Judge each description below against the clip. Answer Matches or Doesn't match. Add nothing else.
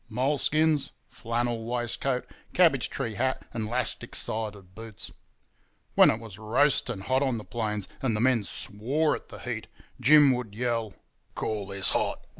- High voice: Doesn't match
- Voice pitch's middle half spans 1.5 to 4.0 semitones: Matches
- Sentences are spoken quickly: Doesn't match